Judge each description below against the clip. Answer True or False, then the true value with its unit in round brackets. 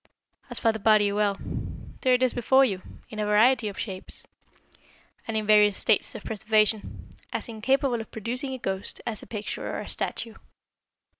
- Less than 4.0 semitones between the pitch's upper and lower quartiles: True (2.7 semitones)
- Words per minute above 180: False (175 wpm)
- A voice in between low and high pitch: False (220 Hz)